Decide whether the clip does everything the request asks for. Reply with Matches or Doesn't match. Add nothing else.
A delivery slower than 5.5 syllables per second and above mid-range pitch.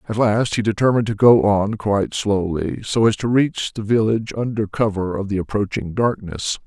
Doesn't match